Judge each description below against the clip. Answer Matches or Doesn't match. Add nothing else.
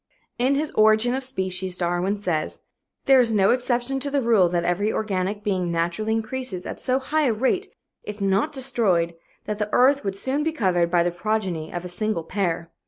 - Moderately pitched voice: Doesn't match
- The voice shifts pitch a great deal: Matches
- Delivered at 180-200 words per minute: Matches